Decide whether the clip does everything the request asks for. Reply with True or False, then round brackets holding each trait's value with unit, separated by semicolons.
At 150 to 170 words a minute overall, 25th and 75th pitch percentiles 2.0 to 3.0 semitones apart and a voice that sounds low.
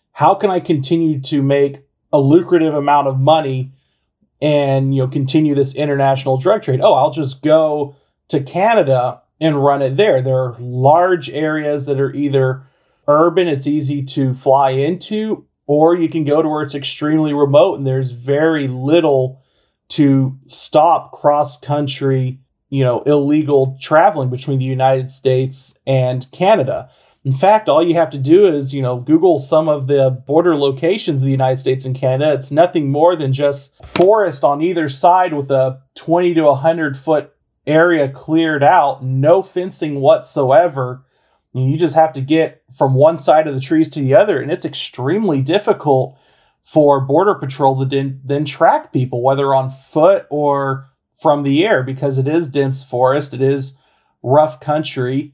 False (165 wpm; 2.7 semitones; 145 Hz)